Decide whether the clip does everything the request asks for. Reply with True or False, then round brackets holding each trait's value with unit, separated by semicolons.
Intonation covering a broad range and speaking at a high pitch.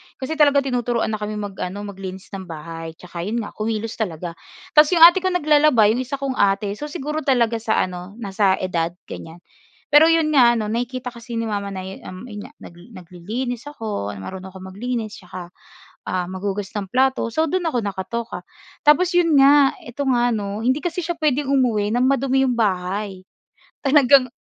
True (5.8 semitones; 230 Hz)